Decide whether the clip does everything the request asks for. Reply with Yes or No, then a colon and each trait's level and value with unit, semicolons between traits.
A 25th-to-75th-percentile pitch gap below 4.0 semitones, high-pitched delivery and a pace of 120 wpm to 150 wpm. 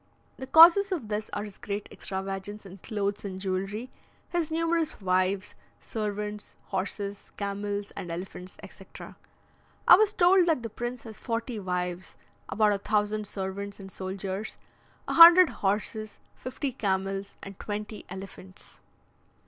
Yes: average, 3.2 semitones; high, 205 Hz; slow, 135 wpm